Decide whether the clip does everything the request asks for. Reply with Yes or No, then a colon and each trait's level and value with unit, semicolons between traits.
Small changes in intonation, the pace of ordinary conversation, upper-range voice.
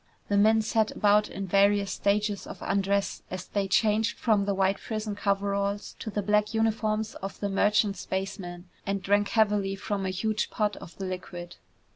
Yes: narrow, 1.4 semitones; average, 175 wpm; high, 200 Hz